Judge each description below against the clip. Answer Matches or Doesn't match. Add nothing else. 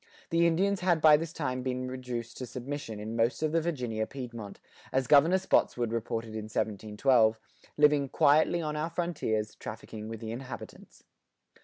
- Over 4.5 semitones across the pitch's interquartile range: Matches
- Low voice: Matches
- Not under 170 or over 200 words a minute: Doesn't match